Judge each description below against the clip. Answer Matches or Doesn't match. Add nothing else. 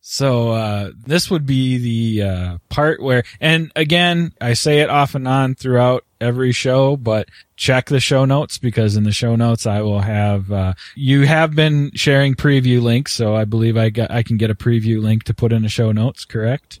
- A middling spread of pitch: Matches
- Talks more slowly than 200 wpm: Doesn't match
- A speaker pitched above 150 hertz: Doesn't match